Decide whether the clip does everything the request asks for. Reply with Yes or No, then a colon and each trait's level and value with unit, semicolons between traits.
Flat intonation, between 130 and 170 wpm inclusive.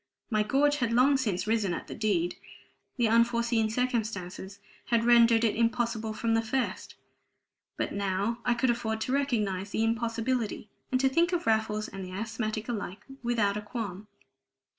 Yes: narrow, 2.3 semitones; average, 160 wpm